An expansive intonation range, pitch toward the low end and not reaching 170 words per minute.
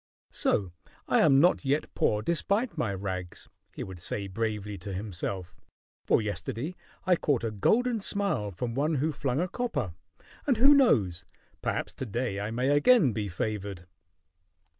Yes: wide, 8.3 semitones; low, 115 Hz; average, 160 wpm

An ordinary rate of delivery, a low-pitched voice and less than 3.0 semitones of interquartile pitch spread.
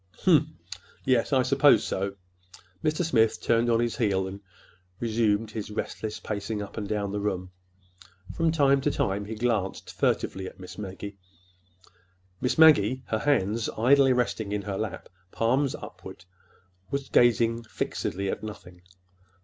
No: average, 145 wpm; low, 110 Hz; average, 3.7 semitones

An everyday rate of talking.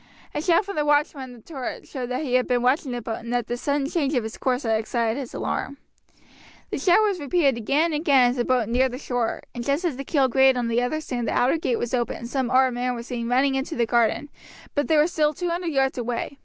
No: fast, 265 wpm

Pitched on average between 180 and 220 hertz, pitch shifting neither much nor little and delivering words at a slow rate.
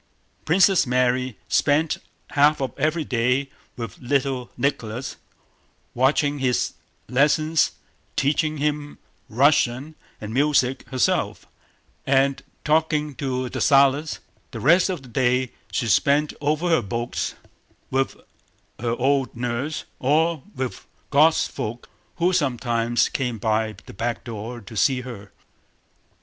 No: low, 135 Hz; average, 3.5 semitones; slow, 115 wpm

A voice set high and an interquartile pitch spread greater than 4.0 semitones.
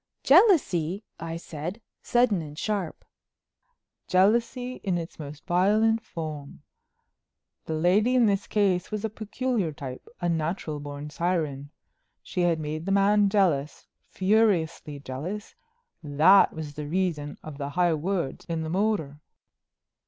No: medium, 175 Hz; average, 5.2 semitones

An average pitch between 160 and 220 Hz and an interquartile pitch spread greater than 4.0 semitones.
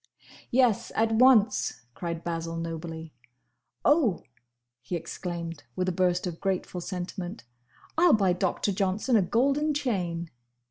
Yes: medium, 185 Hz; average, 4.8 semitones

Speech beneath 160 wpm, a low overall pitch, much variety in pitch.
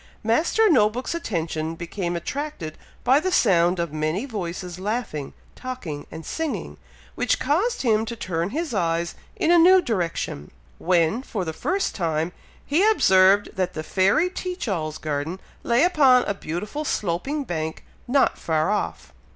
No: average, 150 wpm; high, 195 Hz; wide, 8.6 semitones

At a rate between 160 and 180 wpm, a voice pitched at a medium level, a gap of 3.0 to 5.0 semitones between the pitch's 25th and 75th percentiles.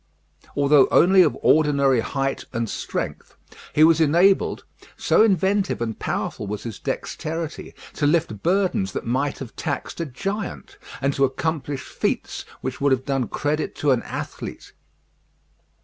No: average, 145 wpm; medium, 145 Hz; average, 4.0 semitones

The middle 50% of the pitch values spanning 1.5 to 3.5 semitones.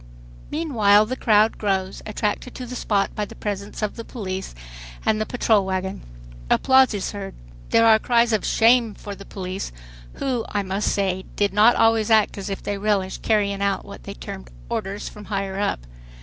Yes: narrow, 2.4 semitones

